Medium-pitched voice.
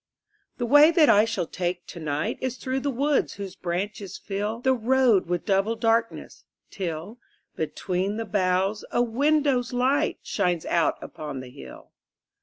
No: high, 210 Hz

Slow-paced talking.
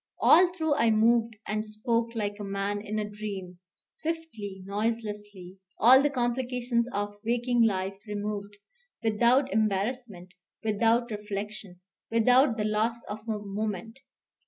Yes: slow, 130 wpm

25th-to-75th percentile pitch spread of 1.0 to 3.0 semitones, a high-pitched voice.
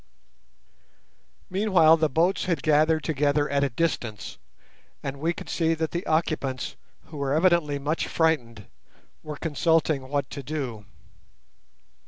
No: narrow, 2.6 semitones; medium, 155 Hz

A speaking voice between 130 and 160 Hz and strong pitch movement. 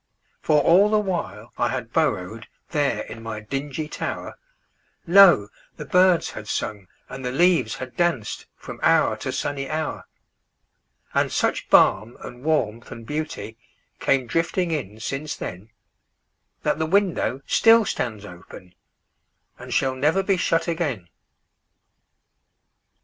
Yes: low, 135 Hz; wide, 7.0 semitones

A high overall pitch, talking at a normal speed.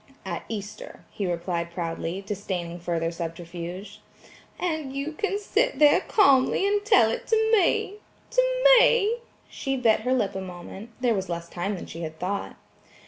Yes: high, 205 Hz; average, 155 wpm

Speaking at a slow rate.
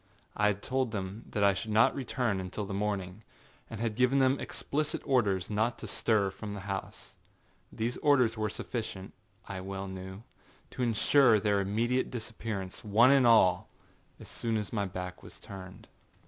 No: average, 170 wpm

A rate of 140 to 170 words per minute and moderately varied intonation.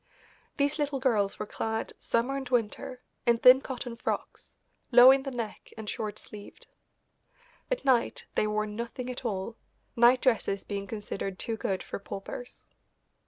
Yes: average, 155 wpm; average, 3.3 semitones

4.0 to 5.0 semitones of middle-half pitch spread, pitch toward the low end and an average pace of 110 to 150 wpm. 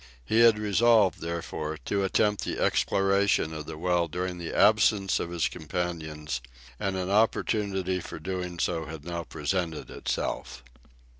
No: average, 3.2 semitones; very low, 90 Hz; average, 145 wpm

